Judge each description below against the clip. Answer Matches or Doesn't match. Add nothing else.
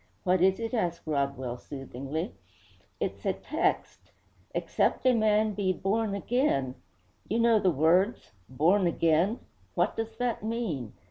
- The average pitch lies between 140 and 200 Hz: Matches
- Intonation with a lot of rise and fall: Matches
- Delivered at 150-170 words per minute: Doesn't match